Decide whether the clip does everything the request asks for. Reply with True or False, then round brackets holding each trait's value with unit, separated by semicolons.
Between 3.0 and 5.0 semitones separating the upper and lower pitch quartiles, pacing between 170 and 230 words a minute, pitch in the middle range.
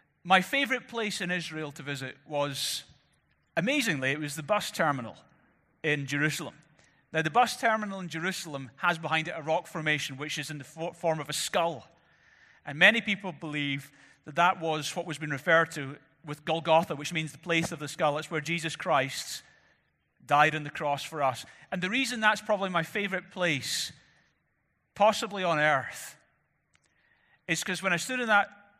True (4.0 semitones; 175 wpm; 160 Hz)